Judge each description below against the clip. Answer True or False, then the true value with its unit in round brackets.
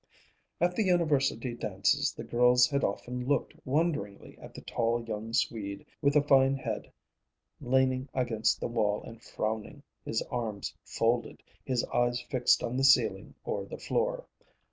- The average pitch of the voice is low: True (125 Hz)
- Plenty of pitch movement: False (3.4 semitones)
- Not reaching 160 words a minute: True (150 wpm)